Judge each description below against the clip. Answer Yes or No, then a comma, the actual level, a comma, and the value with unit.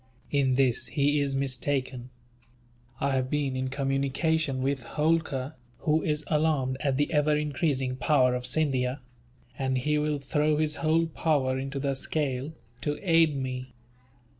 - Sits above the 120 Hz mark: Yes, medium, 140 Hz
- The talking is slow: No, average, 145 wpm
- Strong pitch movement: No, narrow, 2.5 semitones